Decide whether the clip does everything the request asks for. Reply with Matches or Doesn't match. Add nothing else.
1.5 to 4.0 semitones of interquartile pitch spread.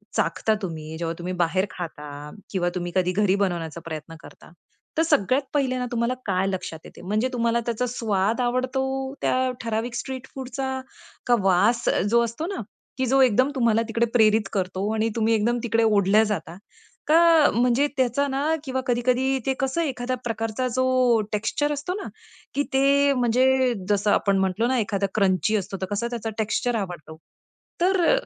Doesn't match